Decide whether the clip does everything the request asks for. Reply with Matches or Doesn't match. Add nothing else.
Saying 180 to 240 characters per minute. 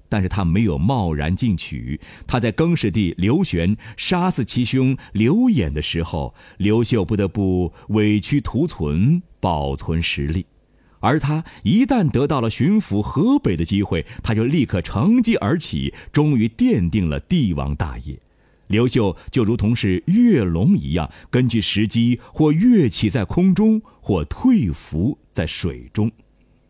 Matches